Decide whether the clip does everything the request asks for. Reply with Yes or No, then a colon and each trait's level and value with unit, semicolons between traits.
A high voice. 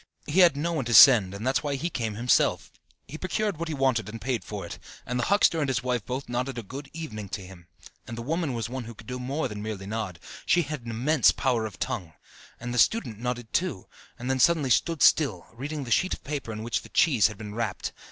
No: low, 125 Hz